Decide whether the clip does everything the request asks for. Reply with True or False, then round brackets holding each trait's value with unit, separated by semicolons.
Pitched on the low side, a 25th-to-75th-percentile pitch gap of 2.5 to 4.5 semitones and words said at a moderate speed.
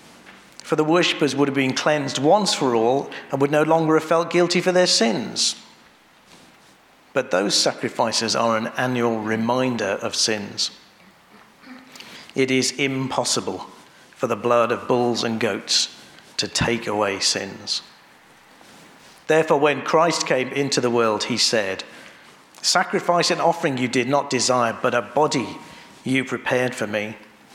False (130 Hz; 4.9 semitones; 145 wpm)